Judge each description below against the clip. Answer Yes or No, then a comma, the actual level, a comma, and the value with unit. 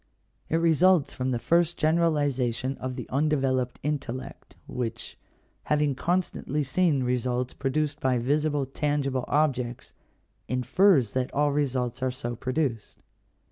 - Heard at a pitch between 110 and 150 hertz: Yes, low, 135 Hz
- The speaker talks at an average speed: No, slow, 120 wpm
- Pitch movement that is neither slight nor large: Yes, average, 3.1 semitones